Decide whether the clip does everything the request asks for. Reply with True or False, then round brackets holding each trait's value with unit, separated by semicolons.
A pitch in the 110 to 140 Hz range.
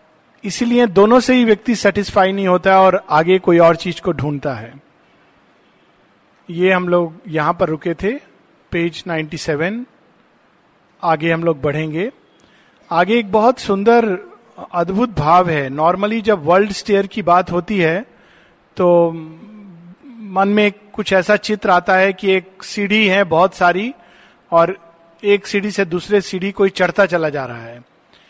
False (185 Hz)